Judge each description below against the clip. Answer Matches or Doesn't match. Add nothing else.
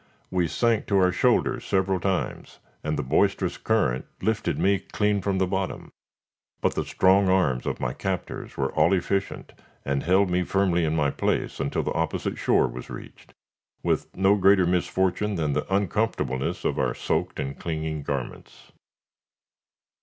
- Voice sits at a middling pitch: Doesn't match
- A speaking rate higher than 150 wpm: Matches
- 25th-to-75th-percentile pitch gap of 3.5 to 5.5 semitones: Matches